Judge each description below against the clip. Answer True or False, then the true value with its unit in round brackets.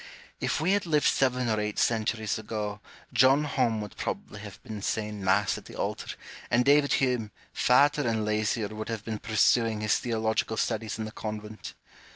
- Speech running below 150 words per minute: False (180 wpm)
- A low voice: True (110 Hz)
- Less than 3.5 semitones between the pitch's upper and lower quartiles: True (2.7 semitones)